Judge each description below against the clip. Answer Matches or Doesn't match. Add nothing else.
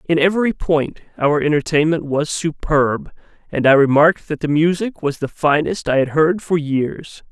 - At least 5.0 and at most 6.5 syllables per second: Doesn't match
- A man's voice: Matches